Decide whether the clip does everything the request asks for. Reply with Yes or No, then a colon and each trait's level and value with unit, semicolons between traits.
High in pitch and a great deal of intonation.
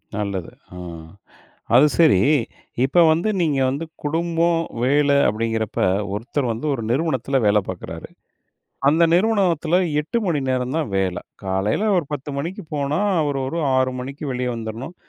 No: medium, 140 Hz; wide, 6.3 semitones